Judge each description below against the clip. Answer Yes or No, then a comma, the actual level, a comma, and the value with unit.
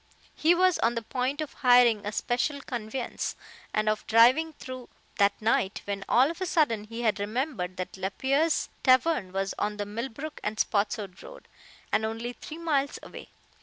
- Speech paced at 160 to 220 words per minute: Yes, average, 170 wpm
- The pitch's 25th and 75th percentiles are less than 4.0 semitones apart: No, average, 5.1 semitones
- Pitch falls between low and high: No, high, 235 Hz